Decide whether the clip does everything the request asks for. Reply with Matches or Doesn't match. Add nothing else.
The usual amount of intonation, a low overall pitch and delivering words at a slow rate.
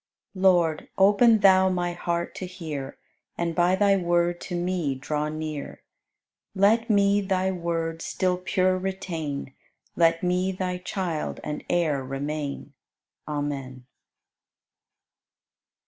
Doesn't match